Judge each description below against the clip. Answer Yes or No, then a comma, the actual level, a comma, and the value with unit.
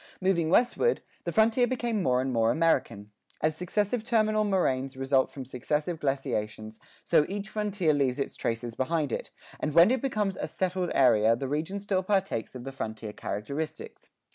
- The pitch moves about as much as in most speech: No, wide, 7.7 semitones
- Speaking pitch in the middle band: Yes, medium, 155 Hz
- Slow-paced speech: No, average, 165 wpm